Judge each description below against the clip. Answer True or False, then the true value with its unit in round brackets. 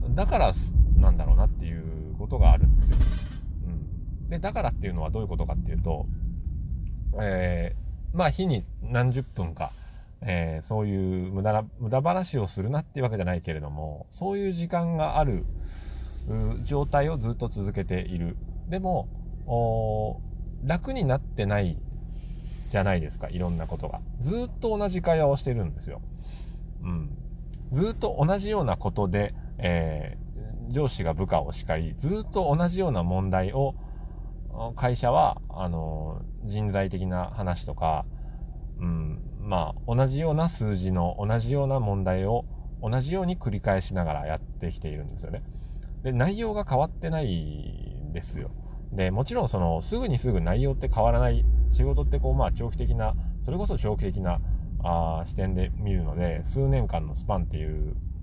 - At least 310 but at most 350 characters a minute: True (320 characters per minute)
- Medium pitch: False (95 Hz)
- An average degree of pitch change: False (7.0 semitones)